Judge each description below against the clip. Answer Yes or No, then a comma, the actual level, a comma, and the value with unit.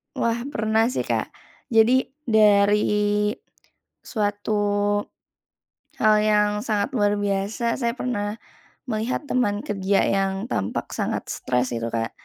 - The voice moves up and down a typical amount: No, narrow, 2.2 semitones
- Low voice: No, high, 210 Hz